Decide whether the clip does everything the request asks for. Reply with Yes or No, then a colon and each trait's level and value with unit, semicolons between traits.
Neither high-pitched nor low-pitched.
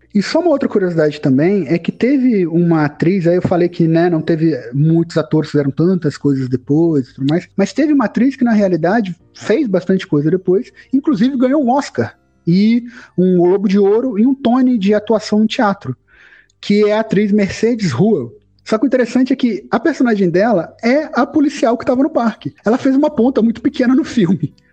No: high, 205 Hz